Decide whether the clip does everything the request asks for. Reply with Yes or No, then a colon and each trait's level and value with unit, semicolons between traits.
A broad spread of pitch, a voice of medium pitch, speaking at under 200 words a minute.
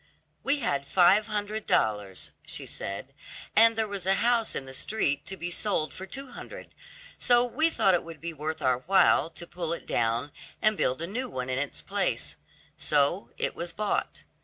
Yes: wide, 7.2 semitones; medium, 175 Hz; average, 190 wpm